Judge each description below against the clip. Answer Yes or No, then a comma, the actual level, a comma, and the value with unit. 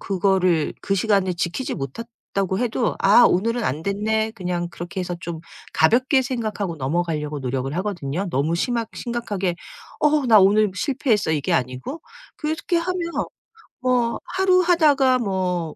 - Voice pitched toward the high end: Yes, high, 200 Hz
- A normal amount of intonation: No, wide, 6.0 semitones